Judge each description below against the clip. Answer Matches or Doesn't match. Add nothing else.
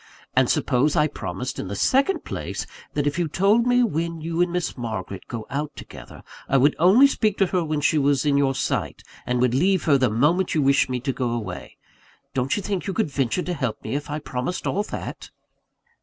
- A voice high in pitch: Doesn't match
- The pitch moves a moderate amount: Doesn't match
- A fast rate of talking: Matches